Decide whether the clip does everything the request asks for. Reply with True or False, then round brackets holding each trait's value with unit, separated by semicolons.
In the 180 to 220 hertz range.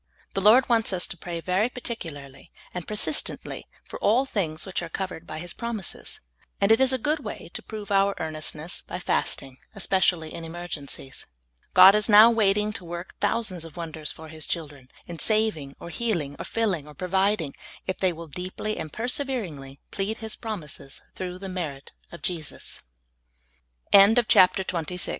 True (185 Hz)